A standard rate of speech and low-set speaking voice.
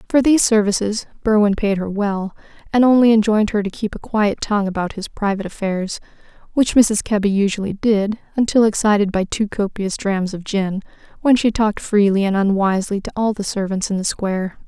No: average, 190 wpm; high, 205 Hz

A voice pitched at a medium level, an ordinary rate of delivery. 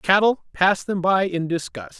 Yes: medium, 175 Hz; average, 180 wpm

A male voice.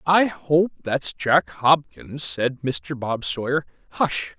Yes: male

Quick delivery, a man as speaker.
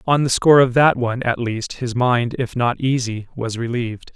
Yes: fast, 215 wpm; male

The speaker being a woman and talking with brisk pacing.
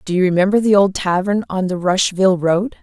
Yes: female; fast, 210 wpm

